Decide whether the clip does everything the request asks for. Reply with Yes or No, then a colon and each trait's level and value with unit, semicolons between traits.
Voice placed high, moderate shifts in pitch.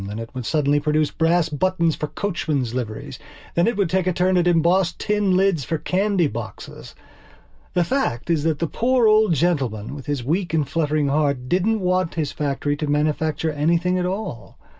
No: medium, 165 Hz; average, 4.0 semitones